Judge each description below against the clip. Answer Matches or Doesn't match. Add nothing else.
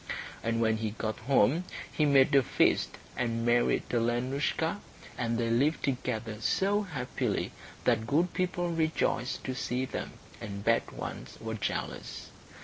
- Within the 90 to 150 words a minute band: Matches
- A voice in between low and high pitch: Doesn't match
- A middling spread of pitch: Matches